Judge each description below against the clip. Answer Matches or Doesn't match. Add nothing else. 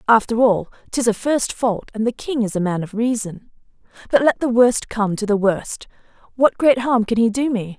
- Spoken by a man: Doesn't match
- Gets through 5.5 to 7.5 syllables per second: Doesn't match